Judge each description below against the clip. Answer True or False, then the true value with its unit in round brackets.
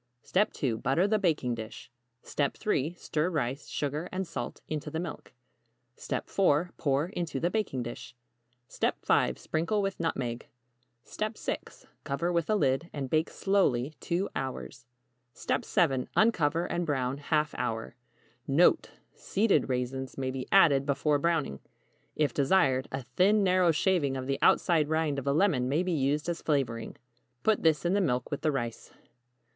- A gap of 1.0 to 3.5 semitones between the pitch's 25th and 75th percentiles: False (4.8 semitones)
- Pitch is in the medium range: True (150 Hz)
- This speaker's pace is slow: False (150 wpm)